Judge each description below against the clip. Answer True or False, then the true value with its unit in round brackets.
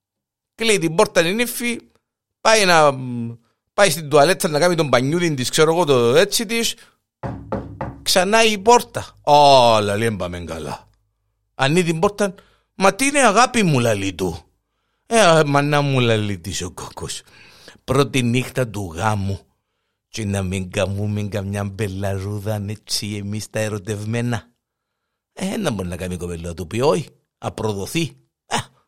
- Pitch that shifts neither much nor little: False (8.4 semitones)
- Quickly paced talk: False (140 wpm)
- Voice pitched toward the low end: True (115 Hz)